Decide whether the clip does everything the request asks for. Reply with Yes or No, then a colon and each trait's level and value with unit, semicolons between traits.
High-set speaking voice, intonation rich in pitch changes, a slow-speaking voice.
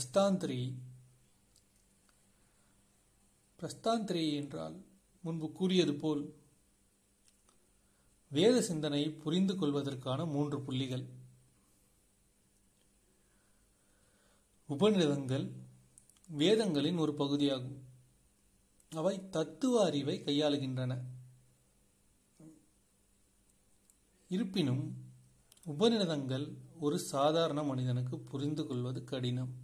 No: low, 135 Hz; wide, 7.4 semitones; slow, 50 wpm